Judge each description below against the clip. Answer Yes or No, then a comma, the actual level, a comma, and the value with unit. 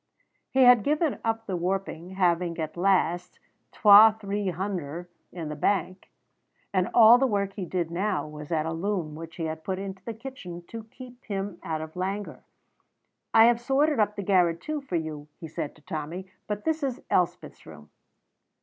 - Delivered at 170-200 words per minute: Yes, average, 185 wpm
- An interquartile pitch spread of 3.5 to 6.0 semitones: Yes, average, 4.6 semitones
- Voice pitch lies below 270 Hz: Yes, high, 190 Hz